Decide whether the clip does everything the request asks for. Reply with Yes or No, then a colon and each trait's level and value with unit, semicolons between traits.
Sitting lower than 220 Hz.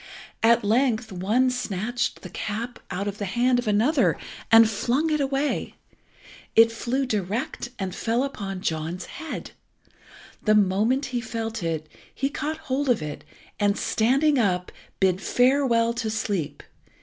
No: high, 225 Hz